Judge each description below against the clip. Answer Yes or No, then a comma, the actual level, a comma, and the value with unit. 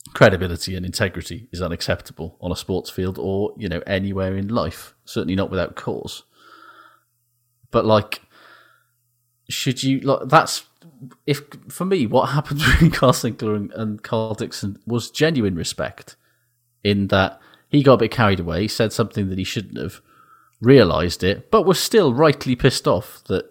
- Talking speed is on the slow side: No, average, 165 wpm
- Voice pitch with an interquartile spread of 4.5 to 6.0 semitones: Yes, average, 4.9 semitones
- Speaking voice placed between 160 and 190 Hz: No, low, 115 Hz